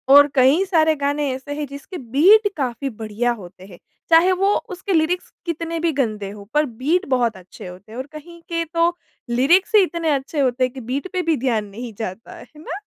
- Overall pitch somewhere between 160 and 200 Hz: No, very high, 280 Hz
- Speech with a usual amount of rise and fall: No, wide, 5.9 semitones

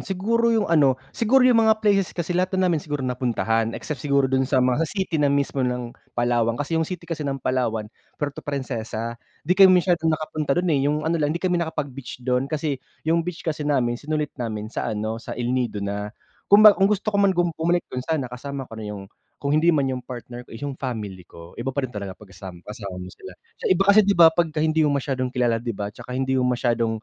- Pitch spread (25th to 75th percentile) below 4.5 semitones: No, wide, 5.5 semitones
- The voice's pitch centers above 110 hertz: Yes, medium, 140 Hz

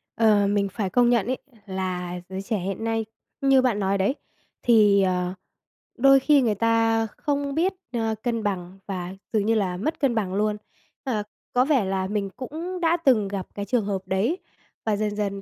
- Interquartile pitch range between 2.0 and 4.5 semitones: Yes, average, 4.1 semitones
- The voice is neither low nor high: No, high, 215 Hz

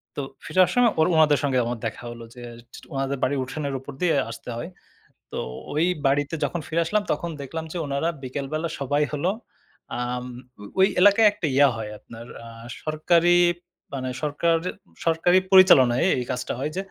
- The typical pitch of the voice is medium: Yes, medium, 145 Hz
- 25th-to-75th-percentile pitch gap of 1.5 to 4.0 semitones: No, average, 4.4 semitones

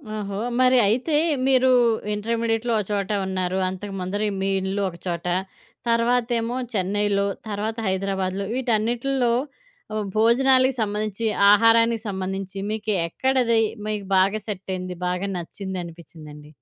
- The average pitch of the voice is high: Yes, high, 205 Hz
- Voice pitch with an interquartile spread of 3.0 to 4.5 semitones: Yes, average, 3.5 semitones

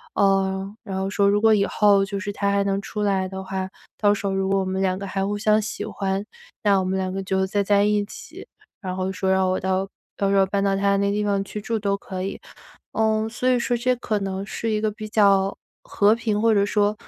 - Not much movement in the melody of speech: Yes, narrow, 1.5 semitones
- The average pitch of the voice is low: No, high, 200 Hz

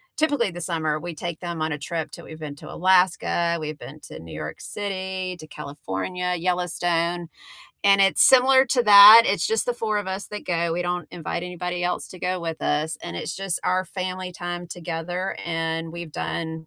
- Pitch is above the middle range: No, medium, 175 Hz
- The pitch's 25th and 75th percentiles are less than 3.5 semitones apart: Yes, narrow, 2.5 semitones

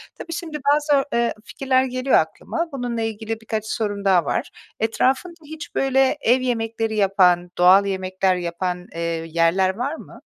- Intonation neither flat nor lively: No, wide, 5.8 semitones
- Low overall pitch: No, high, 225 Hz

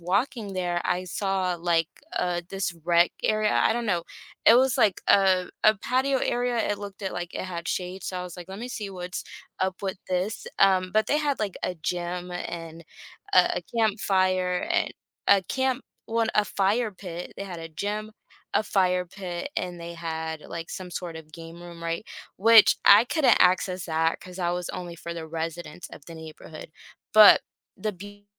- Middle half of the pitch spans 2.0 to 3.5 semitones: Yes, average, 3.2 semitones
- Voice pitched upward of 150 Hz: Yes, medium, 185 Hz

